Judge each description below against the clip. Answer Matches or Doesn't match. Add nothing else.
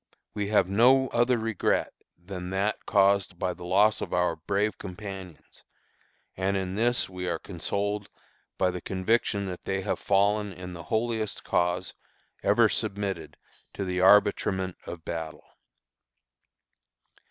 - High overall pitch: Doesn't match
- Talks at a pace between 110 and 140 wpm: Matches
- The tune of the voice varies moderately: Doesn't match